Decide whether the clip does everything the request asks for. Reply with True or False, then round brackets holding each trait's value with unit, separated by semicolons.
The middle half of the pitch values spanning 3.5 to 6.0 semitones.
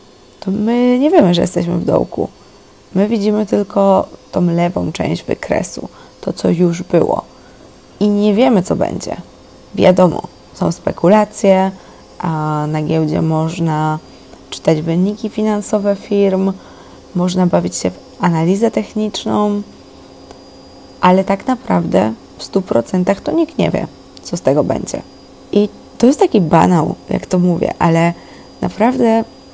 True (3.9 semitones)